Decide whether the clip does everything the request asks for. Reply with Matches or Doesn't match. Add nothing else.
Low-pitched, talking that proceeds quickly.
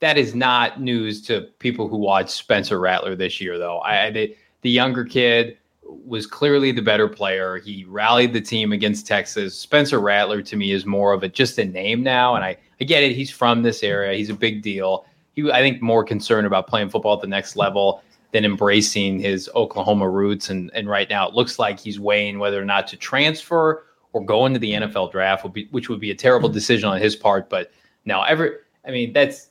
Matches